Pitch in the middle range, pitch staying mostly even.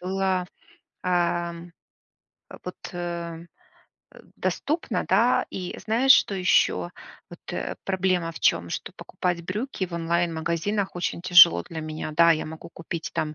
Yes: medium, 175 Hz; narrow, 1.9 semitones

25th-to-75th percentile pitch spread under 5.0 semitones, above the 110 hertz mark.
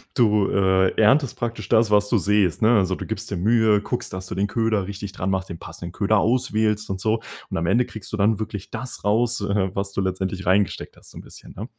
No: narrow, 2.6 semitones; low, 105 Hz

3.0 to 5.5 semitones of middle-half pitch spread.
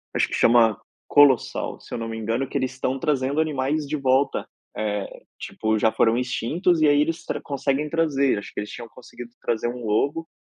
Yes: average, 4.1 semitones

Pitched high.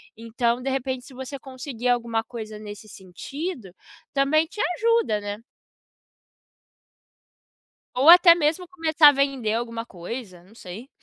Yes: very high, 250 Hz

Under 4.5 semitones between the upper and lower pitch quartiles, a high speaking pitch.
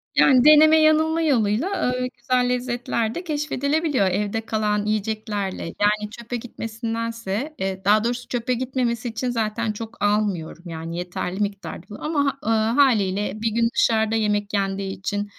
Yes: average, 3.5 semitones; high, 225 Hz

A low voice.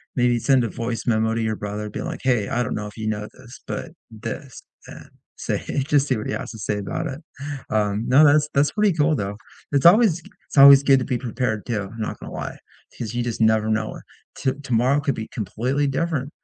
Yes: low, 120 Hz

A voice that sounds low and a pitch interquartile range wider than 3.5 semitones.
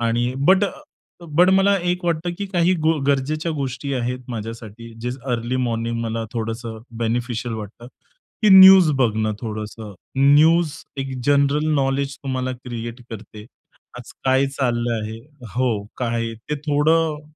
Yes: low, 130 Hz; average, 4.6 semitones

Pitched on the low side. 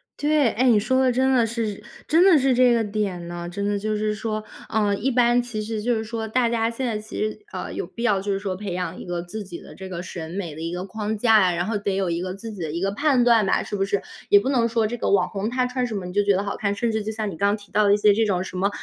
No: high, 210 Hz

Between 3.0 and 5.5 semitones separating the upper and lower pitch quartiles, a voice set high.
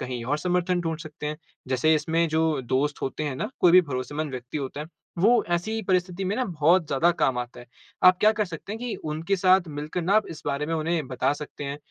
No: average, 3.9 semitones; medium, 160 Hz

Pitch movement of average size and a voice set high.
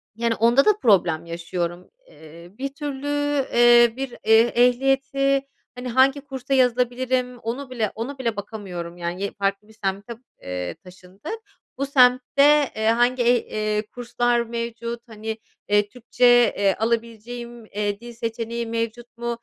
Yes: average, 3.2 semitones; high, 235 Hz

